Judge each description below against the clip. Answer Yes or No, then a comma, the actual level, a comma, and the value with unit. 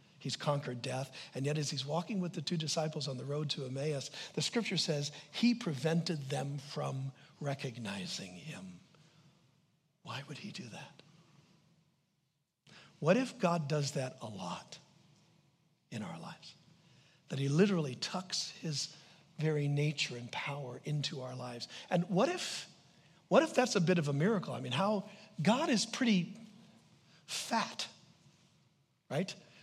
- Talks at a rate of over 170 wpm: No, average, 145 wpm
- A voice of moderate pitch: Yes, medium, 160 Hz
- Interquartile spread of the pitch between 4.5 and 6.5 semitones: No, average, 3.8 semitones